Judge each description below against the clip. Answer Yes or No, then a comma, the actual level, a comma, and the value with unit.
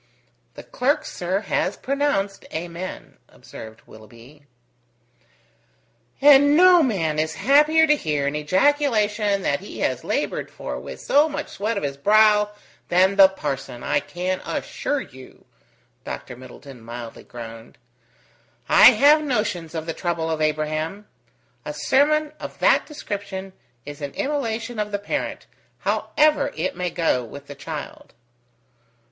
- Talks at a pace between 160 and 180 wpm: No, slow, 135 wpm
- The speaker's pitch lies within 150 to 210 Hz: Yes, high, 190 Hz